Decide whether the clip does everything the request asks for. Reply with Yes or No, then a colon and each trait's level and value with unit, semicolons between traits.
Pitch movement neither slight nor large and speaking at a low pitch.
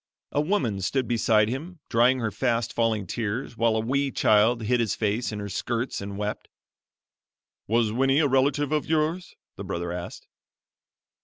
Yes: average, 4.0 semitones; low, 115 Hz